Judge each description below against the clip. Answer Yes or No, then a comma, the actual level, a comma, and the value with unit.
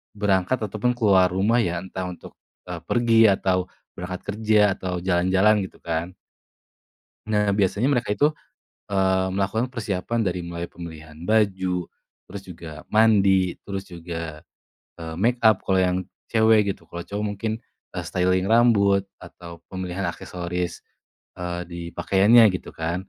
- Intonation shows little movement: No, average, 3.1 semitones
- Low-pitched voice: Yes, very low, 95 Hz